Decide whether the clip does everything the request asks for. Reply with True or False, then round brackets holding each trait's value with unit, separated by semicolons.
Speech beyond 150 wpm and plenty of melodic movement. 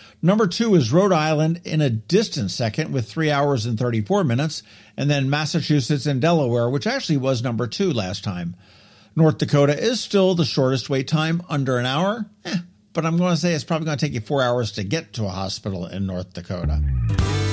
True (205 wpm; 6.4 semitones)